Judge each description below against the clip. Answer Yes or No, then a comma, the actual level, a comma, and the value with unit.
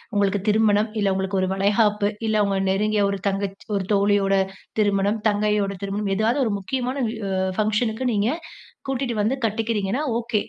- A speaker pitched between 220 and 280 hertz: No, high, 210 Hz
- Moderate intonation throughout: No, narrow, 1.8 semitones